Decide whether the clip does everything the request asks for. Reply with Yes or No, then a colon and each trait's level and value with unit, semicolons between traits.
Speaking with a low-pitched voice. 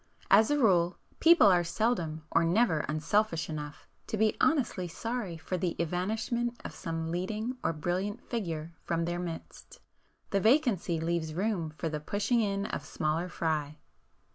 No: medium, 175 Hz